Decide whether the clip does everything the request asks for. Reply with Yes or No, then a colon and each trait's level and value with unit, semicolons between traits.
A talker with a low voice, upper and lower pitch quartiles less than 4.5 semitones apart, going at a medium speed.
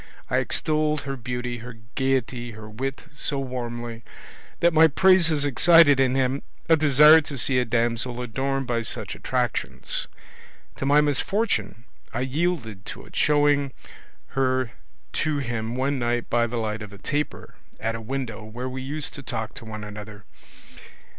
Yes: low, 130 Hz; average, 3.7 semitones; average, 160 wpm